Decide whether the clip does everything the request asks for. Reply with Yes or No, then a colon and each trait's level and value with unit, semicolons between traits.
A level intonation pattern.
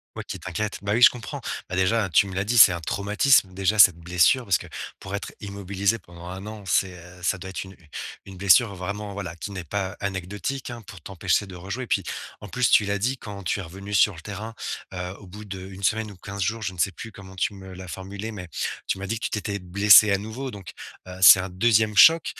Yes: narrow, 2.3 semitones